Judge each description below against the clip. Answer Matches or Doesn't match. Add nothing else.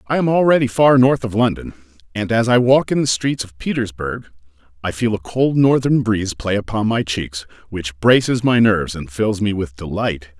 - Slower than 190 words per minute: Doesn't match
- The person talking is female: Doesn't match